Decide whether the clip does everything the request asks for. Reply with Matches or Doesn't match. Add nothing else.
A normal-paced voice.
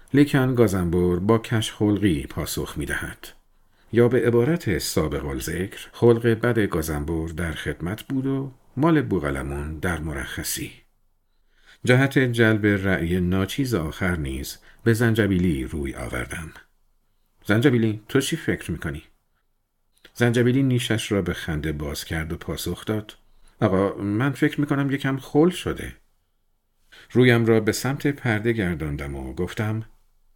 Matches